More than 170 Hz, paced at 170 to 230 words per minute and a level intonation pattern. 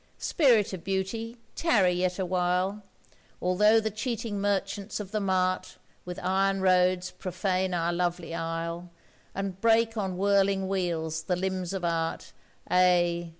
No: medium, 185 Hz; slow, 135 wpm; narrow, 2.0 semitones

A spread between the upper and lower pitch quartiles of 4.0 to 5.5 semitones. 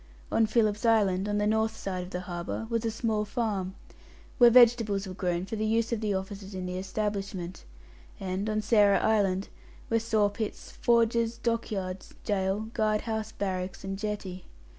No: narrow, 2.6 semitones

